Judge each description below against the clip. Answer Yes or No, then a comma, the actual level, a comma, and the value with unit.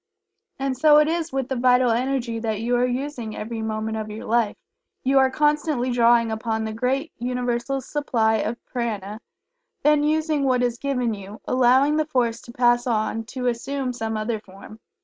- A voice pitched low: No, high, 245 Hz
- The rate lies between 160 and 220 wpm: Yes, average, 180 wpm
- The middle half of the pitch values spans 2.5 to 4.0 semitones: Yes, average, 3.2 semitones